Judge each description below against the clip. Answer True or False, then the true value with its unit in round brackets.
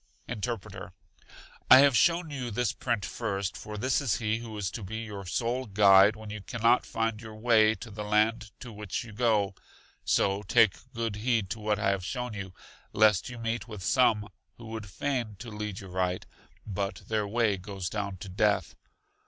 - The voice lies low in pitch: True (110 Hz)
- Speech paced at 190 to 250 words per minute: True (195 wpm)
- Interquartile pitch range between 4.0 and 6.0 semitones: False (2.7 semitones)